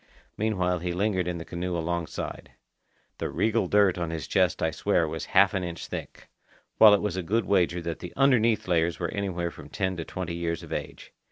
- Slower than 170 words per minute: No, fast, 205 wpm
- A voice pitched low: Yes, very low, 90 Hz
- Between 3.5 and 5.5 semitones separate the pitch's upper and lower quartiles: No, average, 2.9 semitones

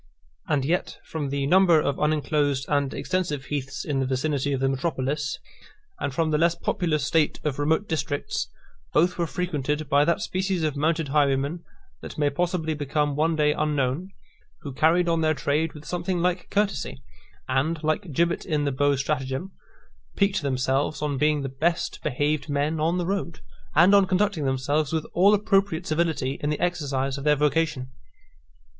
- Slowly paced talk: No, average, 170 wpm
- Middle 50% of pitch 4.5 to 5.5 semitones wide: No, average, 3.2 semitones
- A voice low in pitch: No, medium, 150 Hz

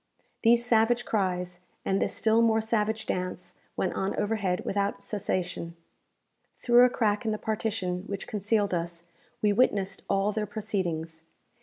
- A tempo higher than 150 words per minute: No, average, 145 wpm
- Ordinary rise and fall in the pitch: Yes, average, 3.3 semitones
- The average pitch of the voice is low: No, high, 205 Hz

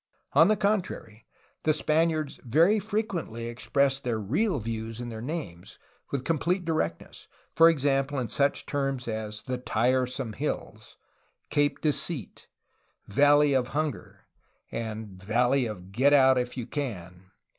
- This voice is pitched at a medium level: No, low, 130 Hz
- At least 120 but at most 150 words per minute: Yes, slow, 135 wpm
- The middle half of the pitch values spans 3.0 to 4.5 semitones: No, average, 5.0 semitones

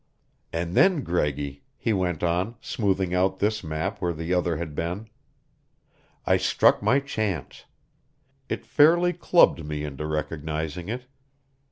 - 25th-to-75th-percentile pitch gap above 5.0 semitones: Yes, wide, 5.6 semitones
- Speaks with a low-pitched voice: Yes, very low, 90 Hz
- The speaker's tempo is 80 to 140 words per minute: Yes, slow, 135 wpm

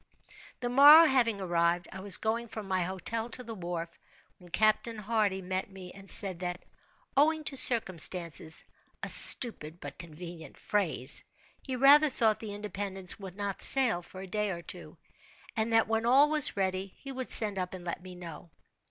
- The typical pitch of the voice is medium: No, high, 195 Hz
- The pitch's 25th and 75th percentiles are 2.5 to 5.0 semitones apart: Yes, average, 4.4 semitones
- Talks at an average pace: Yes, average, 180 wpm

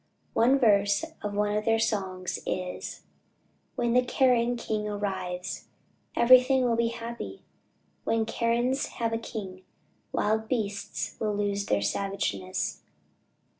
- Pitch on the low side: No, high, 220 Hz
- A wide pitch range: No, average, 2.8 semitones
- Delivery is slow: Yes, slow, 125 wpm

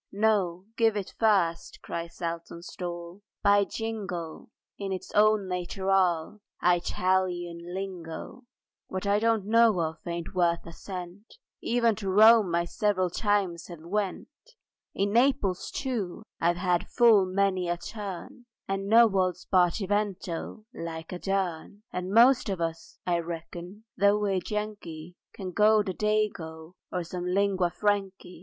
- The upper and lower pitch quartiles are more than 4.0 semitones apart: No, average, 3.2 semitones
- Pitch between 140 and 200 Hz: Yes, high, 190 Hz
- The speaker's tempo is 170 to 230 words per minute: No, slow, 135 wpm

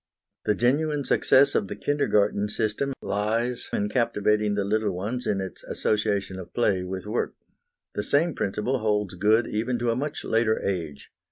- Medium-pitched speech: No, low, 105 Hz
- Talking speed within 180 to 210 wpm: No, average, 165 wpm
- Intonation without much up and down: No, average, 3.2 semitones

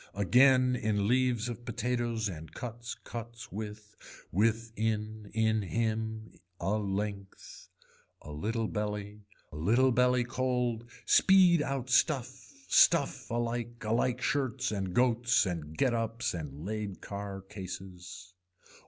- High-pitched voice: No, low, 110 Hz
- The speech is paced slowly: Yes, slow, 120 wpm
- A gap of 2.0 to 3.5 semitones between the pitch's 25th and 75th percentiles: Yes, average, 3.1 semitones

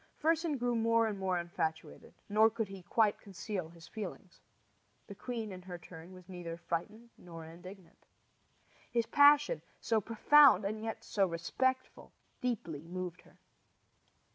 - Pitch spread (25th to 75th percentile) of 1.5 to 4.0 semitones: No, average, 4.5 semitones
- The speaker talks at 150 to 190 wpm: No, average, 140 wpm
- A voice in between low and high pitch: No, high, 200 Hz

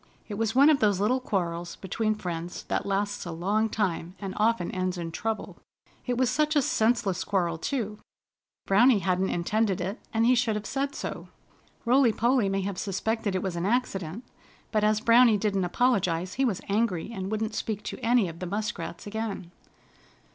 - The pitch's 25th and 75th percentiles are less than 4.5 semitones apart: Yes, average, 3.7 semitones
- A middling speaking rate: Yes, average, 185 wpm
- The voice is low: No, high, 210 Hz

